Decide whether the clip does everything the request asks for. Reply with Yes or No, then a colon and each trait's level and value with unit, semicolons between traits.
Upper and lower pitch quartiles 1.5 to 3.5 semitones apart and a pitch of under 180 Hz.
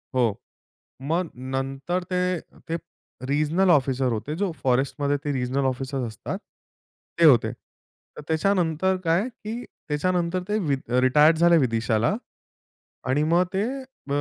No: average, 5.0 semitones; medium, 150 Hz